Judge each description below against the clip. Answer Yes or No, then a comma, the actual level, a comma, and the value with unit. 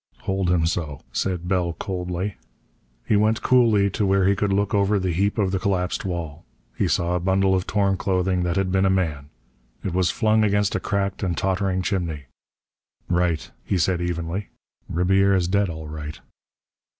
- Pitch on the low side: Yes, very low, 95 Hz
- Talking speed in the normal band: Yes, average, 175 wpm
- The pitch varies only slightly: Yes, narrow, 2.1 semitones